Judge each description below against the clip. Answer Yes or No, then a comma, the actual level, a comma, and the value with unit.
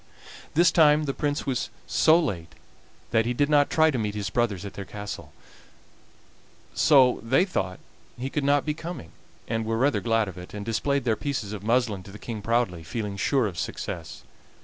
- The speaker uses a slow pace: No, average, 195 wpm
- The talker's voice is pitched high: No, low, 115 Hz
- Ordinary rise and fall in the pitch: No, wide, 5.7 semitones